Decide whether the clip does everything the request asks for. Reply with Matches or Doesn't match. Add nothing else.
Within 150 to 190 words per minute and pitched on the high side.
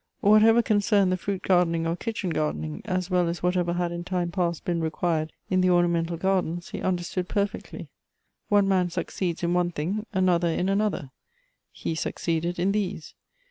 Doesn't match